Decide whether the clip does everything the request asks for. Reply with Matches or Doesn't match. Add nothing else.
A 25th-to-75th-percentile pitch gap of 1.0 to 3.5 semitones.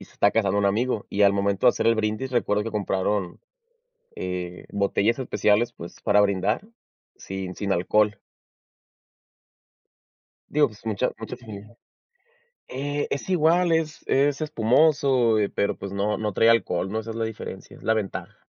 Doesn't match